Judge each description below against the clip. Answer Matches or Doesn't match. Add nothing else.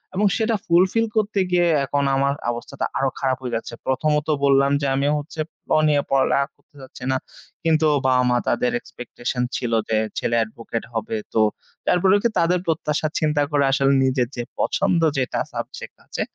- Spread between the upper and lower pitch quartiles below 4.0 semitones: Doesn't match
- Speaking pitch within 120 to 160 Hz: Matches